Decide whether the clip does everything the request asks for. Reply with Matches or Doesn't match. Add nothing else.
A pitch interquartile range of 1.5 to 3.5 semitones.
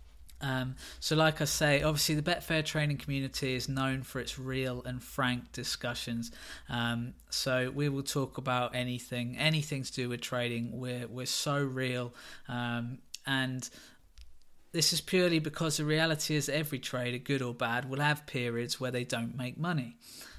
Matches